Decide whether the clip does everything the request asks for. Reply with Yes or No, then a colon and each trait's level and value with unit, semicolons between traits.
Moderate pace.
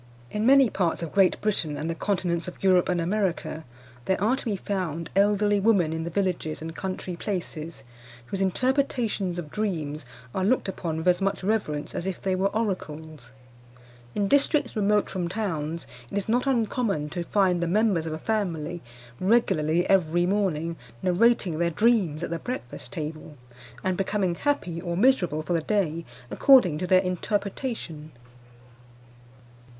Yes: average, 160 wpm